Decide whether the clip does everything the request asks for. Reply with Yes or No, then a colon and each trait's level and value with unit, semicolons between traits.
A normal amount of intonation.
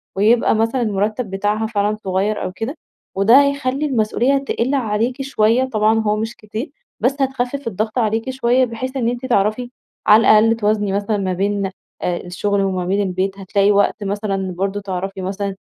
Yes: average, 3.5 semitones